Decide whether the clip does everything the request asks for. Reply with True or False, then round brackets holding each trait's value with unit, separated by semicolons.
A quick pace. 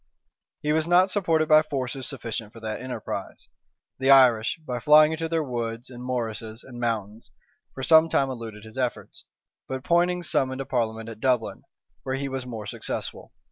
False (175 wpm)